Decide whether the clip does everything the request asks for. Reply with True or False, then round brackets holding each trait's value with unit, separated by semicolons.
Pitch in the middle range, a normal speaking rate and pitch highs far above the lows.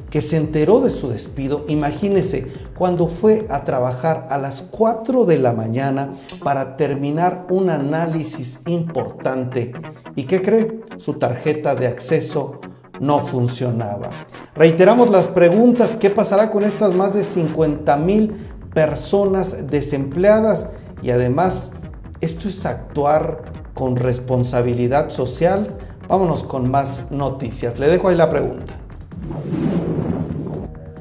False (150 Hz; 120 wpm; 6.0 semitones)